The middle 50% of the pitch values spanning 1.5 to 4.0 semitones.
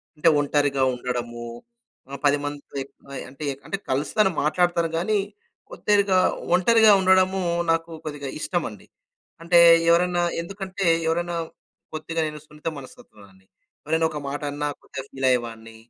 No: average, 4.7 semitones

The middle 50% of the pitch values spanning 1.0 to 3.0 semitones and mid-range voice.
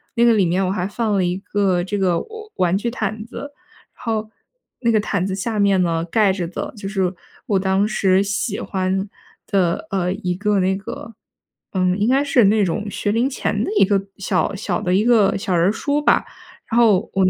No: average, 2.7 semitones; high, 200 Hz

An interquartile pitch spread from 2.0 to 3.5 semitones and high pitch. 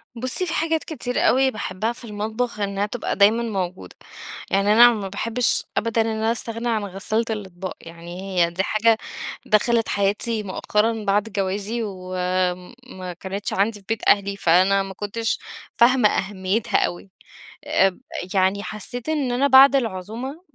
Yes: average, 3.1 semitones; high, 210 Hz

